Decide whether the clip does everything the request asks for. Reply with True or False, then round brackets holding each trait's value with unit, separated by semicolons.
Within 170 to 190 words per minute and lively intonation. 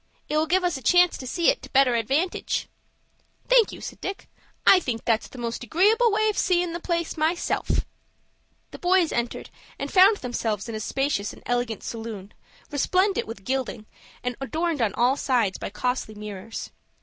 True (180 wpm; 7.5 semitones)